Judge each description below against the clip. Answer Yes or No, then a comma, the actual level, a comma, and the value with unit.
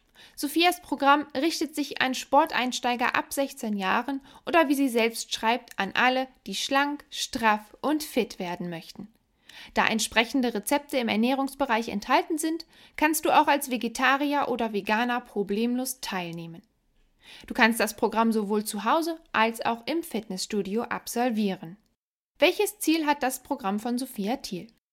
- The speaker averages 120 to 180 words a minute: Yes, average, 140 wpm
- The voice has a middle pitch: No, high, 245 Hz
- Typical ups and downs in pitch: Yes, average, 4.7 semitones